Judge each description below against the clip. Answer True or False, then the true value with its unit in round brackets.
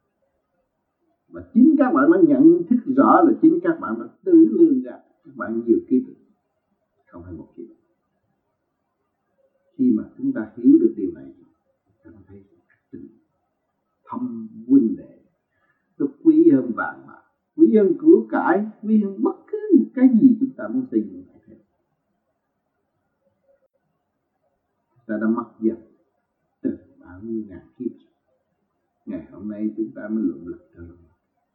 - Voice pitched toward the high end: True (275 Hz)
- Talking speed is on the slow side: True (145 wpm)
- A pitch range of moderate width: False (6.4 semitones)